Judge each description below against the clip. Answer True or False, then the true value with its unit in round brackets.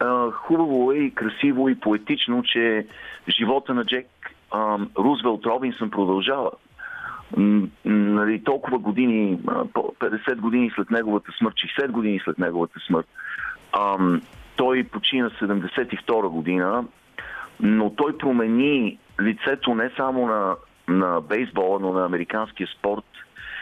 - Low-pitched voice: True (110 Hz)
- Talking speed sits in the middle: False (110 wpm)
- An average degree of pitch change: True (3.9 semitones)